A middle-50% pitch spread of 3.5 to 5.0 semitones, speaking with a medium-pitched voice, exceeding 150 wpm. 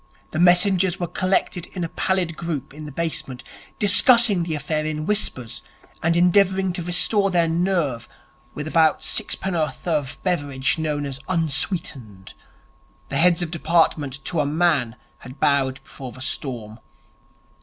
No: average, 4.2 semitones; medium, 160 Hz; average, 145 wpm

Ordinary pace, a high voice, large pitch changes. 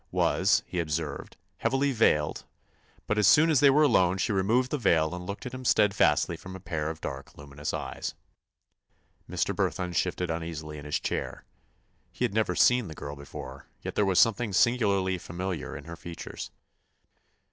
No: average, 175 wpm; very low, 90 Hz; wide, 6.0 semitones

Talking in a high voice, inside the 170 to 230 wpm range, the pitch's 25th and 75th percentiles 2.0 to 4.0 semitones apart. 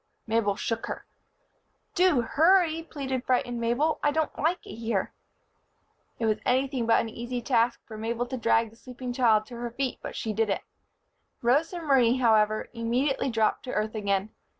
Yes: high, 240 Hz; average, 175 wpm; average, 3.2 semitones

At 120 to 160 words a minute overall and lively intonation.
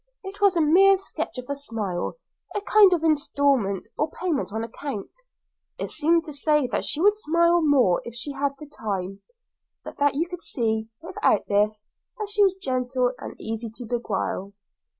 No: average, 175 wpm; wide, 7.2 semitones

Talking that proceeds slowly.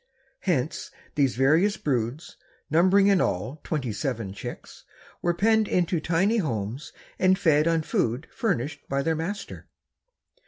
Yes: slow, 130 wpm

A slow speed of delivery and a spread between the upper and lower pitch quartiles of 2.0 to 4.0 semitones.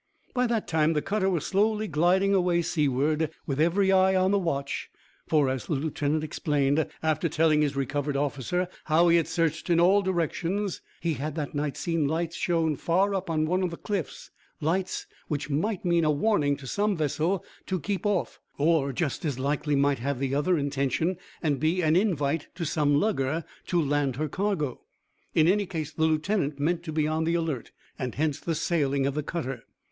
No: average, 195 wpm; average, 3.7 semitones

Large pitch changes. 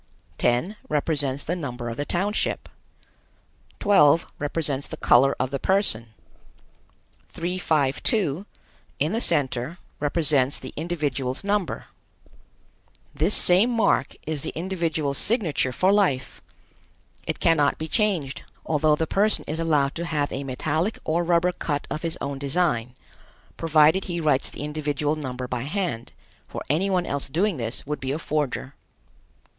No: average, 4.1 semitones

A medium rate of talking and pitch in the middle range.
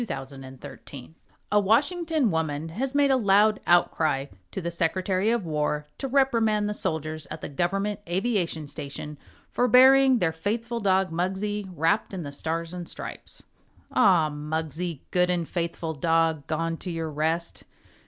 Yes: average, 165 wpm; medium, 175 Hz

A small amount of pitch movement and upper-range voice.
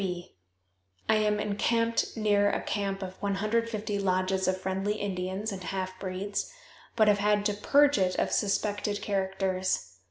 Yes: narrow, 1.8 semitones; high, 200 Hz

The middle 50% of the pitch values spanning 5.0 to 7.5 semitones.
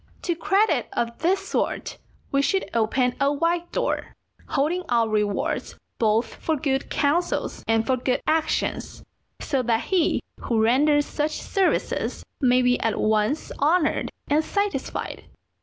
Yes: wide, 5.6 semitones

